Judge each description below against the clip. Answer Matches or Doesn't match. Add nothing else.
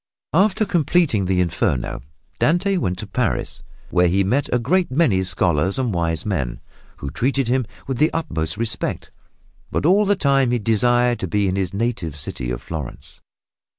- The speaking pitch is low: Matches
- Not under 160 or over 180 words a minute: Matches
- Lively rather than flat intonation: Matches